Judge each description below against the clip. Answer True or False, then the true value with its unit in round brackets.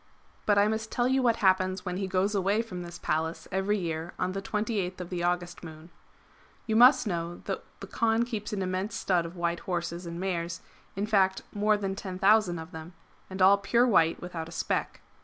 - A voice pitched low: False (190 Hz)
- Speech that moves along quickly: True (210 wpm)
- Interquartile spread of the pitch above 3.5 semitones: False (3.2 semitones)